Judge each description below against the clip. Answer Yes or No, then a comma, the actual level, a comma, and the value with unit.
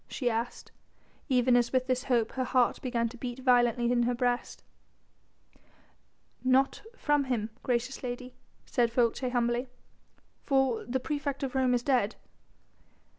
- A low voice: No, very high, 250 Hz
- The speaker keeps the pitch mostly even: Yes, narrow, 1.4 semitones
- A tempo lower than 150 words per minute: Yes, average, 140 wpm